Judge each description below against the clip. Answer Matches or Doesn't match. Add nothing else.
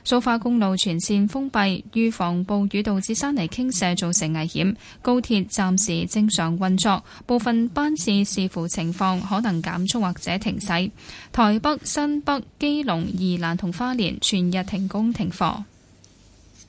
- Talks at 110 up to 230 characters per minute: Matches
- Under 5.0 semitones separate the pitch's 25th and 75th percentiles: Matches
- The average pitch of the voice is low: Doesn't match